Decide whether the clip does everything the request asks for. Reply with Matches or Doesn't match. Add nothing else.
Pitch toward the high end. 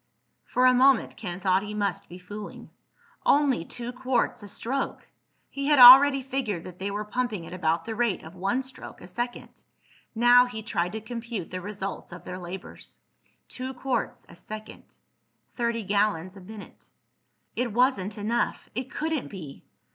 Matches